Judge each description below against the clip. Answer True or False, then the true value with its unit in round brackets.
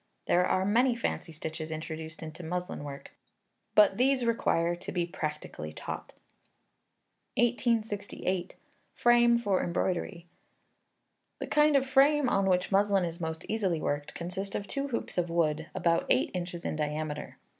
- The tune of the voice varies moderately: False (5.8 semitones)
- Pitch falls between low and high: True (180 Hz)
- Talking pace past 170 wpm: False (145 wpm)